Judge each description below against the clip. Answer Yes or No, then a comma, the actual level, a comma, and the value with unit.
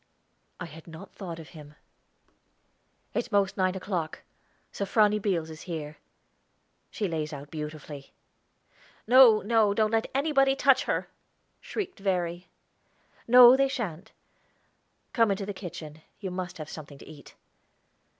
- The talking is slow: Yes, slow, 130 wpm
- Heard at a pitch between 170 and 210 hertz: Yes, high, 190 Hz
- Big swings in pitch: Yes, wide, 5.8 semitones